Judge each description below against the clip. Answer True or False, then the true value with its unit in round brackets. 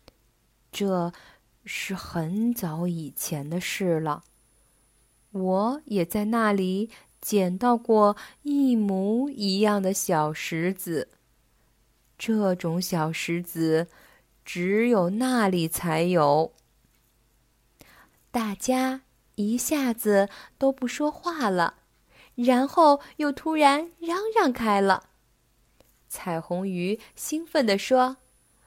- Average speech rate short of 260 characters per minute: True (130 characters per minute)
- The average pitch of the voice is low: False (200 Hz)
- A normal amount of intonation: False (6.3 semitones)